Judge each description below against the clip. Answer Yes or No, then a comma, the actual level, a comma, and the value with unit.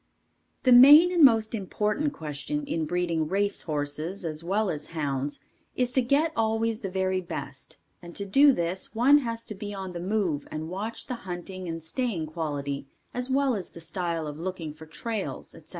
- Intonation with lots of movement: Yes, wide, 6.1 semitones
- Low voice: No, high, 190 Hz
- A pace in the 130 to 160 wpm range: No, average, 185 wpm